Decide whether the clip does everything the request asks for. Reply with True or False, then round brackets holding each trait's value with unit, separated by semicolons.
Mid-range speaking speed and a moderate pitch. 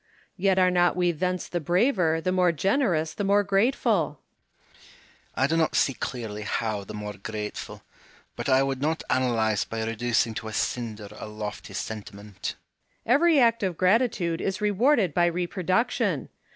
True (170 wpm; 165 Hz)